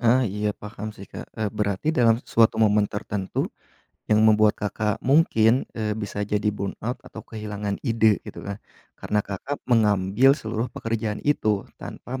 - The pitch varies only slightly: Yes, narrow, 1.7 semitones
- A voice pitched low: Yes, low, 105 Hz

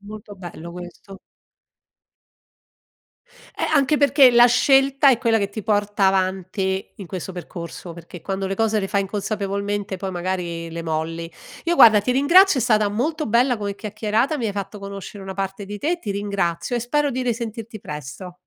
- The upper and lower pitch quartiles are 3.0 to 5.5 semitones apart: Yes, average, 4.0 semitones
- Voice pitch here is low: No, high, 205 Hz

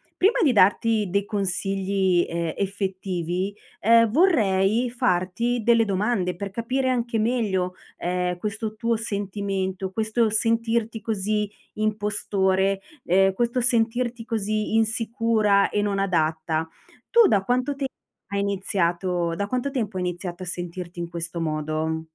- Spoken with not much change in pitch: No, average, 3.7 semitones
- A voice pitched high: Yes, high, 200 Hz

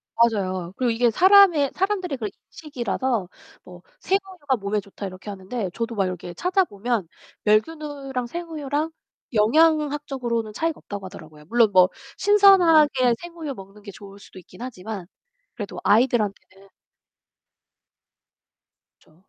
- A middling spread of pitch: No, wide, 7.4 semitones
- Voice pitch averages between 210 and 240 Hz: Yes, high, 235 Hz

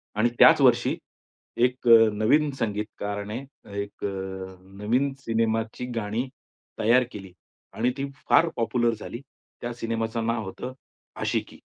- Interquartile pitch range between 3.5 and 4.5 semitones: No, narrow, 2.4 semitones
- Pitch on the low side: Yes, low, 115 Hz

